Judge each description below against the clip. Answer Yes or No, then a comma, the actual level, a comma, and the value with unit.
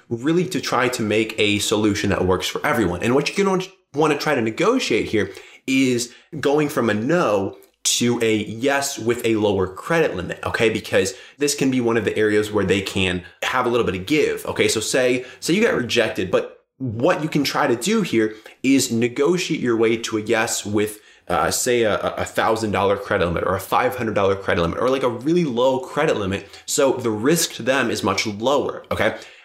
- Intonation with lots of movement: Yes, wide, 6.4 semitones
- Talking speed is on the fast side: Yes, fast, 215 wpm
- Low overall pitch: Yes, low, 125 Hz